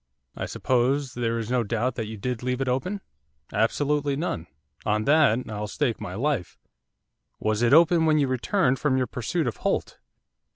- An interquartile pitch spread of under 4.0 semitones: No, average, 4.3 semitones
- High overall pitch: No, low, 125 Hz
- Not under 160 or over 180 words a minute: Yes, average, 175 wpm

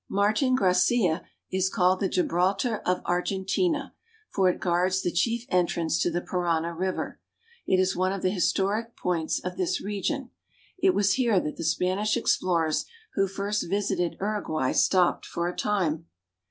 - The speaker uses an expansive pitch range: No, narrow, 2.5 semitones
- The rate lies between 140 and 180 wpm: Yes, average, 160 wpm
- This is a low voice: No, medium, 185 Hz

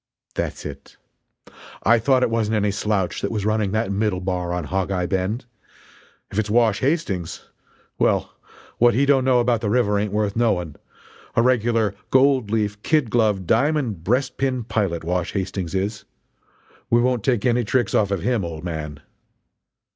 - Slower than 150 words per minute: No, average, 165 wpm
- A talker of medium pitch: No, low, 105 Hz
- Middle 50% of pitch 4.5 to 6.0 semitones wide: No, average, 4.0 semitones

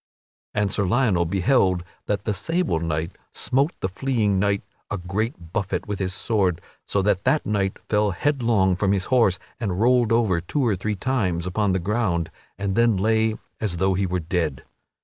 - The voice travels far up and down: No, average, 3.5 semitones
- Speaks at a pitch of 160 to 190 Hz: No, low, 100 Hz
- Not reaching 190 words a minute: Yes, average, 180 wpm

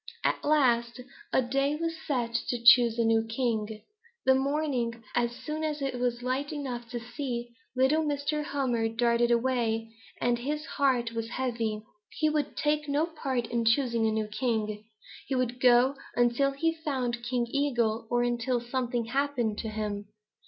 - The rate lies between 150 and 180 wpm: Yes, average, 165 wpm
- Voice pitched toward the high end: Yes, high, 245 Hz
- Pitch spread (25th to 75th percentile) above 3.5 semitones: No, average, 3.0 semitones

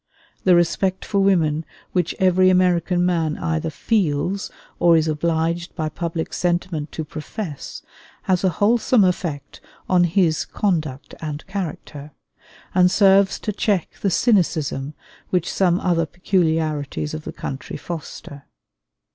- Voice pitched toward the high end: No, medium, 170 Hz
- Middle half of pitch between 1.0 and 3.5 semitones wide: Yes, average, 3.0 semitones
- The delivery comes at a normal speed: No, slow, 130 wpm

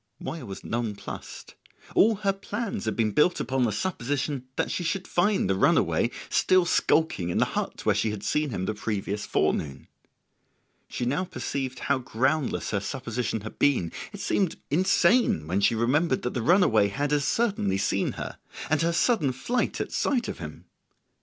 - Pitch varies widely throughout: Yes, wide, 8.3 semitones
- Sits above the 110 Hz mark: Yes, low, 135 Hz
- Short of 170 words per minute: No, average, 175 wpm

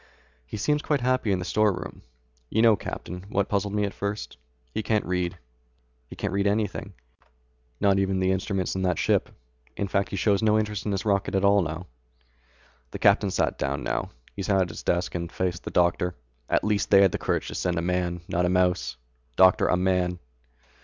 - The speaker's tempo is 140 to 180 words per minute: No, average, 200 wpm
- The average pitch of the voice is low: Yes, very low, 95 Hz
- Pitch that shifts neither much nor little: No, narrow, 2.3 semitones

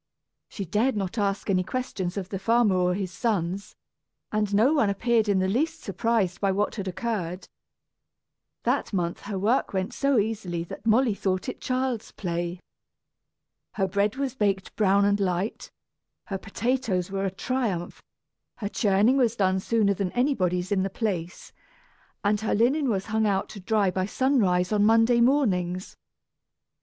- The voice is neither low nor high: No, high, 200 Hz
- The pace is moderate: Yes, average, 160 wpm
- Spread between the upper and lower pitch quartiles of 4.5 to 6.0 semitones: No, average, 3.5 semitones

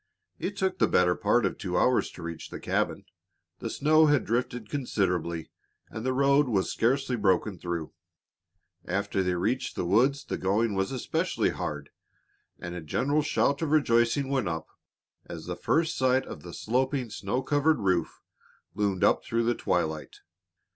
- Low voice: Yes, low, 115 Hz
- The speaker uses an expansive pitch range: Yes, wide, 7.0 semitones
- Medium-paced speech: Yes, average, 165 wpm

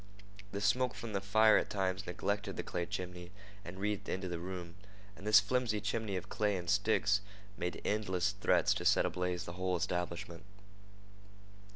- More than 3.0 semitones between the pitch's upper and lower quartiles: No, average, 2.7 semitones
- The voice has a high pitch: No, very low, 95 Hz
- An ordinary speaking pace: Yes, average, 170 wpm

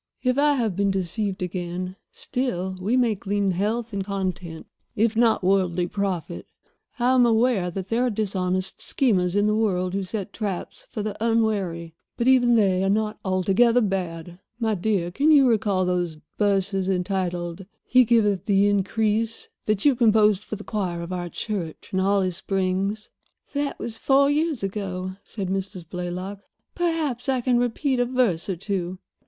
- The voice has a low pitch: No, high, 200 Hz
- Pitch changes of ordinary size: Yes, average, 3.8 semitones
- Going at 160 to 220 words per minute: Yes, average, 165 wpm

